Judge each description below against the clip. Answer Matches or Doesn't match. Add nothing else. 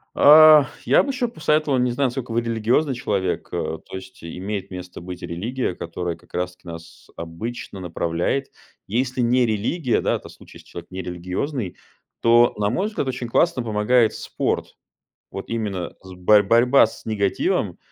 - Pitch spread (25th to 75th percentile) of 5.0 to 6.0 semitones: Matches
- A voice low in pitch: Matches